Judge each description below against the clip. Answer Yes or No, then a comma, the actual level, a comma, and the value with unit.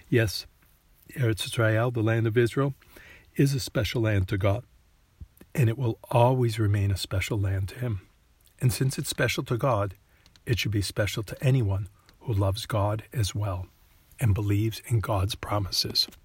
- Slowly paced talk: No, average, 165 wpm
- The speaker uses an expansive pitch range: No, average, 3.7 semitones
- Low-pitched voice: Yes, low, 110 Hz